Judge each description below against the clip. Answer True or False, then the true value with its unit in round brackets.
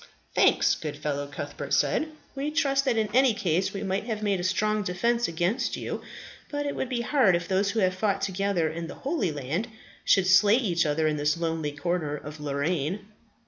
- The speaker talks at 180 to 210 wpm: True (200 wpm)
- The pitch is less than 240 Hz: True (190 Hz)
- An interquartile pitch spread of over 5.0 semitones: True (5.5 semitones)